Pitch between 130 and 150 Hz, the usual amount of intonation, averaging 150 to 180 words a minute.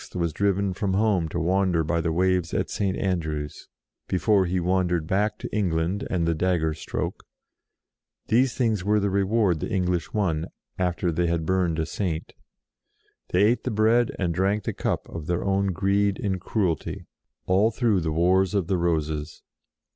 No: very low, 95 Hz; average, 3.1 semitones; average, 170 wpm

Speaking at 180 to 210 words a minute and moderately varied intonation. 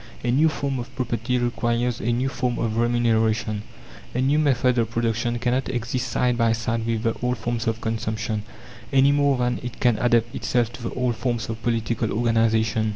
No: average, 190 wpm; narrow, 1.6 semitones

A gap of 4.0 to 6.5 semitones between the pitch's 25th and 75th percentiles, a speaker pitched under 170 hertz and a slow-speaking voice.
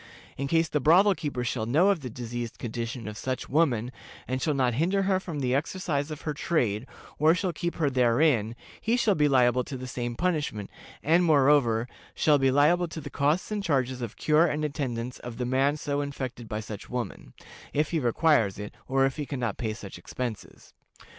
No: average, 4.4 semitones; low, 135 Hz; fast, 205 wpm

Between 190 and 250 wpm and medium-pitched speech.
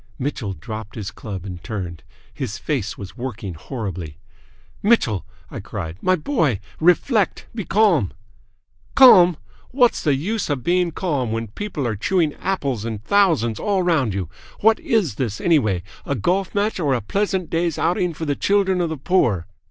No: average, 165 wpm; medium, 145 Hz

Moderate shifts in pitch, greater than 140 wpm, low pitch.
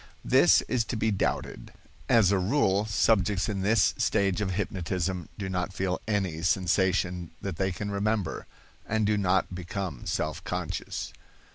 No: narrow, 2.3 semitones; average, 150 wpm; very low, 95 Hz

